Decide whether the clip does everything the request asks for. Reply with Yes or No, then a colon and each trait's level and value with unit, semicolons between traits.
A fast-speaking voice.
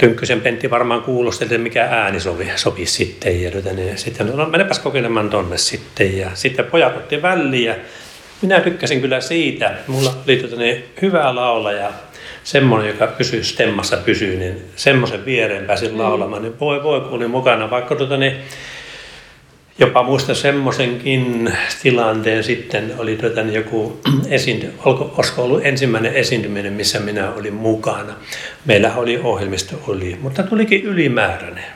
No: average, 140 wpm